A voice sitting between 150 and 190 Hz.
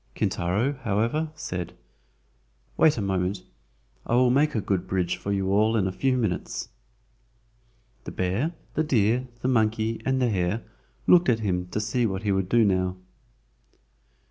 No: low, 110 Hz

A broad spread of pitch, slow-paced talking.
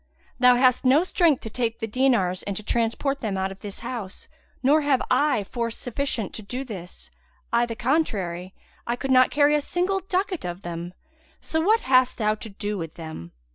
No: wide, 5.7 semitones; average, 195 wpm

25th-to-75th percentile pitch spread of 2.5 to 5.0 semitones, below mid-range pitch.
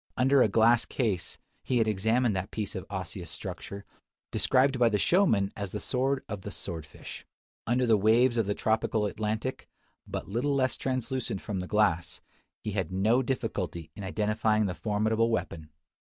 Yes: average, 3.7 semitones; low, 110 Hz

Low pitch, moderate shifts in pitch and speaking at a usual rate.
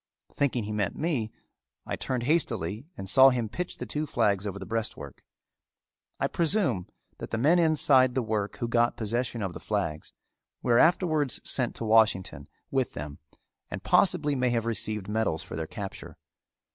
Yes: low, 115 Hz; average, 4.4 semitones; average, 170 wpm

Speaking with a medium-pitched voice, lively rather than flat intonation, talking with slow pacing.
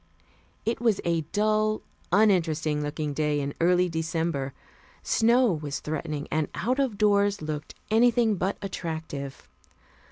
Yes: medium, 170 Hz; wide, 5.8 semitones; slow, 125 wpm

